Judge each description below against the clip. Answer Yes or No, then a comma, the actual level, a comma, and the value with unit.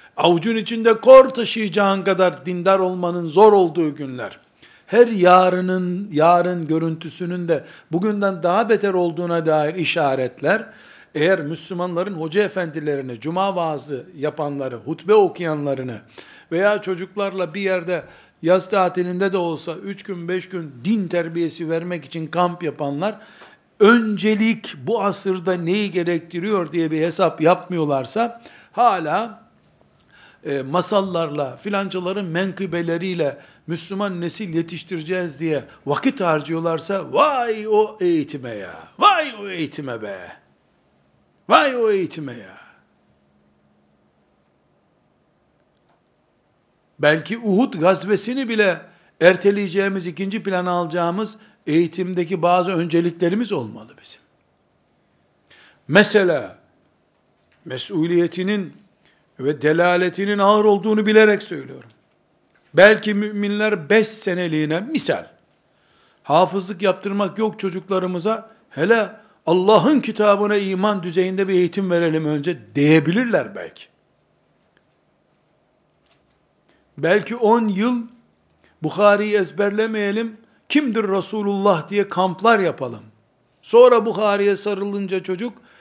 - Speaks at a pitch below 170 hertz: No, medium, 185 Hz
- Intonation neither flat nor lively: Yes, average, 3.9 semitones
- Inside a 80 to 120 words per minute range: Yes, slow, 95 wpm